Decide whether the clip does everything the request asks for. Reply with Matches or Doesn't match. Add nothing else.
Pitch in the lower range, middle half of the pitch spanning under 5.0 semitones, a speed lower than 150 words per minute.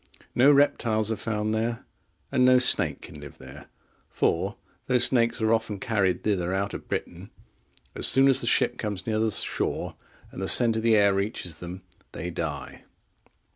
Doesn't match